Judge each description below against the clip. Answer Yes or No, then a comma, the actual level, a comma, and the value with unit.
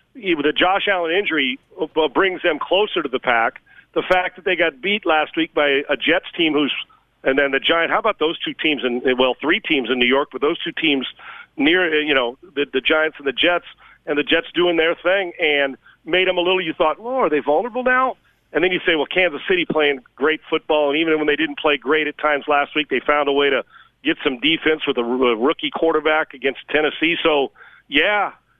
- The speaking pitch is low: No, medium, 155 Hz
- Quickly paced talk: Yes, fast, 230 wpm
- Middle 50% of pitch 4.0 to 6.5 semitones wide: No, average, 3.6 semitones